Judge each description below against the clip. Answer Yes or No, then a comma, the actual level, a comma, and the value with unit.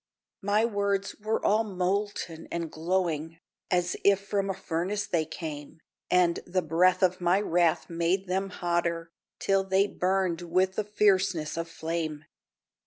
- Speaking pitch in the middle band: Yes, medium, 180 Hz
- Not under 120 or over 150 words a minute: Yes, average, 145 wpm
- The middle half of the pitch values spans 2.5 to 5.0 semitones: Yes, average, 2.8 semitones